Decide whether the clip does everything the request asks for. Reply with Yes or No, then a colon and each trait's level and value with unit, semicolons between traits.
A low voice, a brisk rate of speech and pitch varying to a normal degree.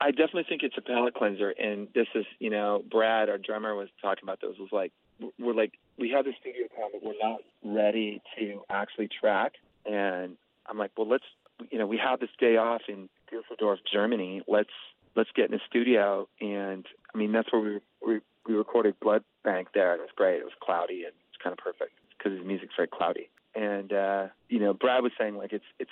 Yes: low, 110 Hz; fast, 220 wpm; average, 3.1 semitones